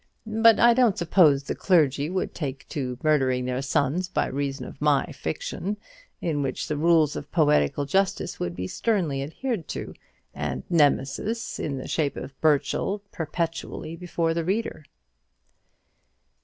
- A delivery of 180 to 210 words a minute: No, average, 145 wpm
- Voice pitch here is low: No, medium, 155 Hz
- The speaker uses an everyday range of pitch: Yes, average, 4.9 semitones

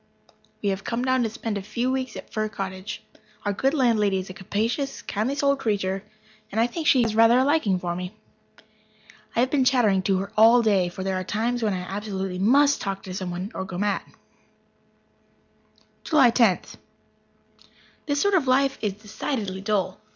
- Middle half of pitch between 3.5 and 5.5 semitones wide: Yes, average, 4.8 semitones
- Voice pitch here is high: Yes, high, 215 Hz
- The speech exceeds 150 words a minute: Yes, average, 185 wpm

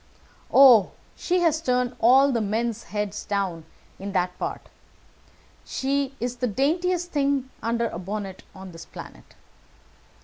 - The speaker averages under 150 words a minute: Yes, slow, 135 wpm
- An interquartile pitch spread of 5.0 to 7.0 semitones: Yes, wide, 5.5 semitones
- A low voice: No, high, 235 Hz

